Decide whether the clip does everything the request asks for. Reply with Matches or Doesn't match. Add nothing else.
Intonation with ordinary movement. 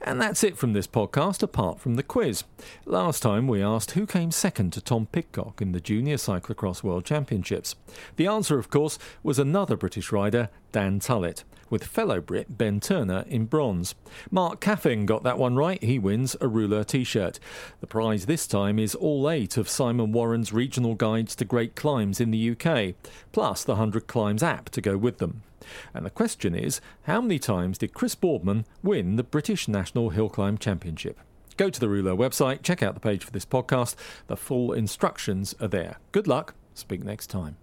Doesn't match